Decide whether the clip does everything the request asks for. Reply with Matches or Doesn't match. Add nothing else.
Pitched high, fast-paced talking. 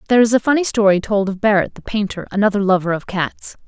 Matches